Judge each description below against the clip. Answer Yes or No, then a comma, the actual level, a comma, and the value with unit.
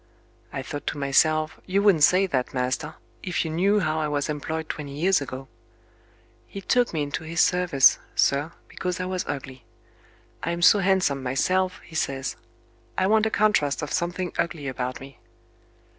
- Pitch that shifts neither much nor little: Yes, average, 4.7 semitones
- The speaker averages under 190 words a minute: Yes, average, 170 wpm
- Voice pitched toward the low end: No, medium, 160 Hz